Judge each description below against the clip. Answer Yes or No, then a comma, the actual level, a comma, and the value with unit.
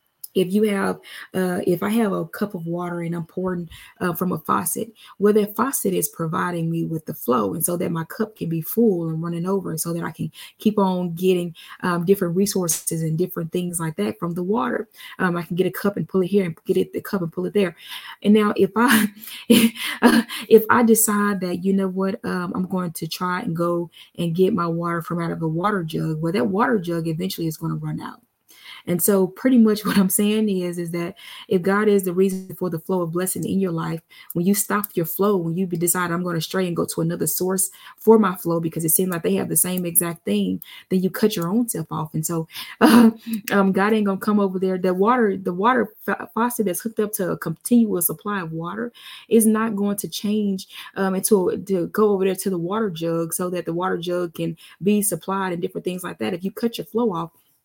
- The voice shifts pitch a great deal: No, average, 3.3 semitones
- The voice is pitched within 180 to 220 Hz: Yes, medium, 185 Hz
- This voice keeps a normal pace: No, fast, 240 wpm